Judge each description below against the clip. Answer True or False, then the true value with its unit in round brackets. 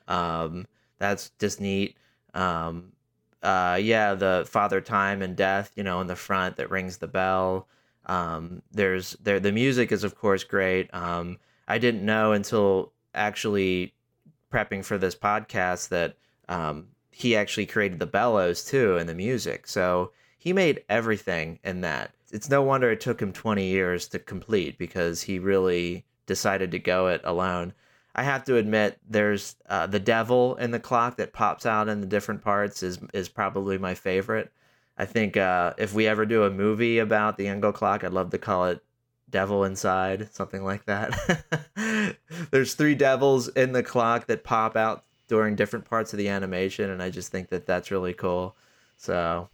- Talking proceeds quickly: False (175 wpm)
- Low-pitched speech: True (100 Hz)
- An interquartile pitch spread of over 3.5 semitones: False (3.1 semitones)